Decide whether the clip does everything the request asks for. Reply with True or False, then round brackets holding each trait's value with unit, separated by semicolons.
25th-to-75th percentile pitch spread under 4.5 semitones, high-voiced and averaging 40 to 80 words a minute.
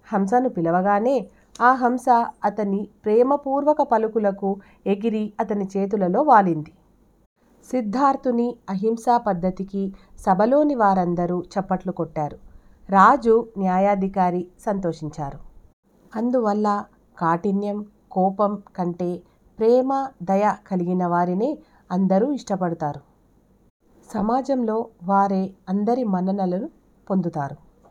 True (3.9 semitones; 200 Hz; 75 wpm)